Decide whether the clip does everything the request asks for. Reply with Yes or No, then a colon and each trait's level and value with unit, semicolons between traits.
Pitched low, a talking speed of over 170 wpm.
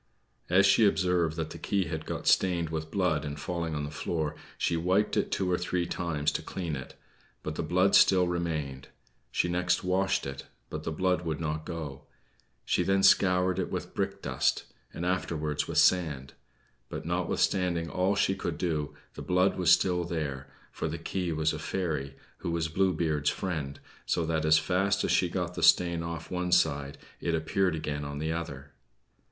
Yes: very low, 85 Hz; average, 185 wpm